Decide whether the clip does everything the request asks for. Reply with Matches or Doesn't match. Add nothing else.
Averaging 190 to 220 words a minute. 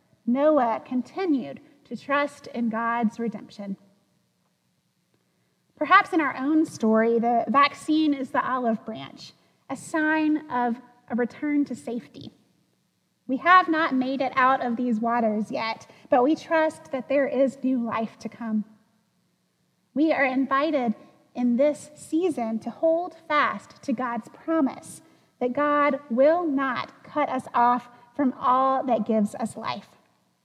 Doesn't match